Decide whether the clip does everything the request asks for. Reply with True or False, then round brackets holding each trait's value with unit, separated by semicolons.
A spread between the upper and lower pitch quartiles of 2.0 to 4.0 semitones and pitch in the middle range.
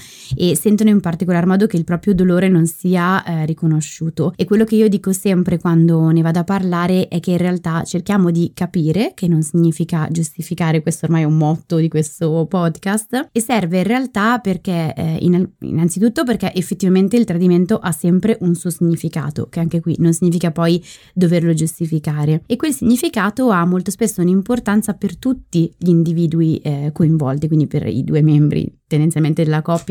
True (2.9 semitones; 175 Hz)